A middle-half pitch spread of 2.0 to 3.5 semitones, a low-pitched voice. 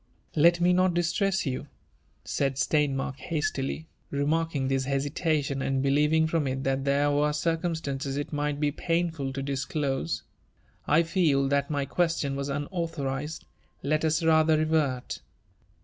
No: average, 2.8 semitones; medium, 145 Hz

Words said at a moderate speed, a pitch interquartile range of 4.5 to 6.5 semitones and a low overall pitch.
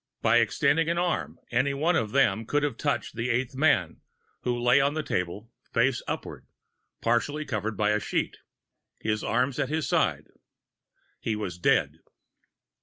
Yes: average, 160 wpm; average, 4.8 semitones; low, 125 Hz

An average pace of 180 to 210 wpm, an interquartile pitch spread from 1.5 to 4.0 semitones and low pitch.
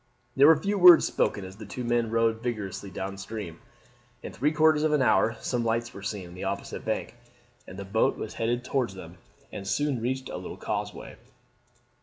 No: average, 200 wpm; average, 5.1 semitones; low, 115 Hz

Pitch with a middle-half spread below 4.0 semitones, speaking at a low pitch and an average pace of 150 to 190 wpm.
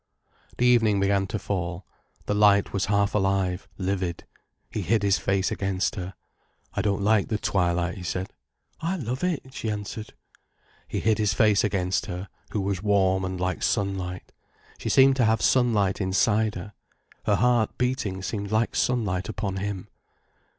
Yes: narrow, 2.6 semitones; low, 100 Hz; average, 165 wpm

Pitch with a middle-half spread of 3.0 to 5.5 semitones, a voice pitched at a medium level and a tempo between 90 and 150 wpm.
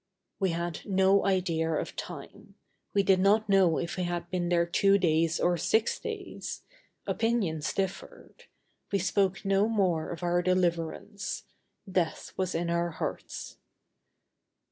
No: narrow, 2.4 semitones; medium, 180 Hz; average, 140 wpm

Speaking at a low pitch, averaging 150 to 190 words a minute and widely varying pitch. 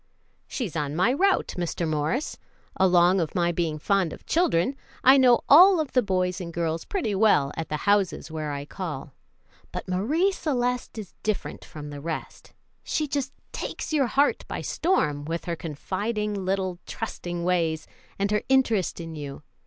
No: medium, 185 Hz; average, 170 wpm; wide, 7.1 semitones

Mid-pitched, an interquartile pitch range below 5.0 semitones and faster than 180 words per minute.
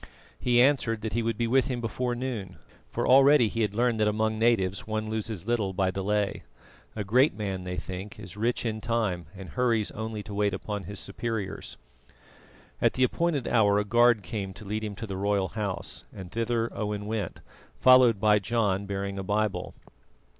No: low, 110 Hz; average, 2.8 semitones; average, 190 wpm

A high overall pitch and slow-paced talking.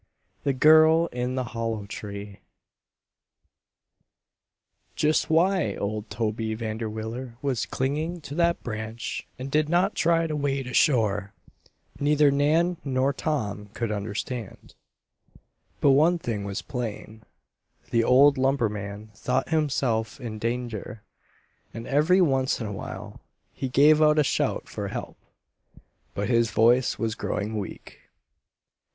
No: low, 125 Hz; slow, 125 wpm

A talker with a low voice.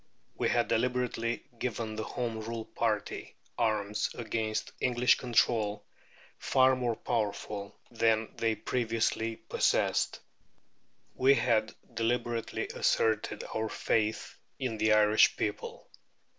Yes: low, 115 Hz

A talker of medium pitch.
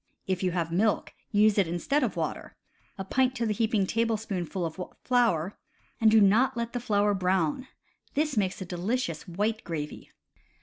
No: high, 205 Hz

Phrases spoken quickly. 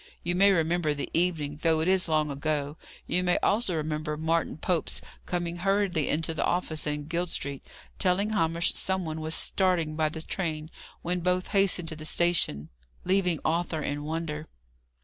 No: average, 170 wpm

